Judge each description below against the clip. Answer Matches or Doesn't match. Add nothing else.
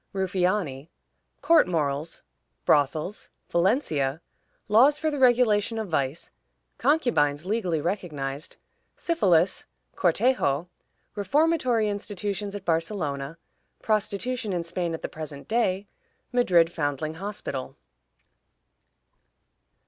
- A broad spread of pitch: Matches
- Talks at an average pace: Doesn't match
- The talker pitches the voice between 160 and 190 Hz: Matches